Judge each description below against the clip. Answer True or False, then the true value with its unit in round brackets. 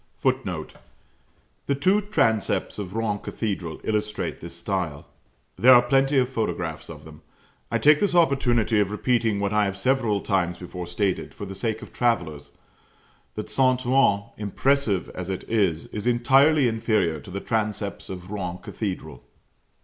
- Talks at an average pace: True (155 wpm)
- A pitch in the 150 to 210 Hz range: False (105 Hz)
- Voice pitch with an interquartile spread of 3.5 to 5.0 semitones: True (4.6 semitones)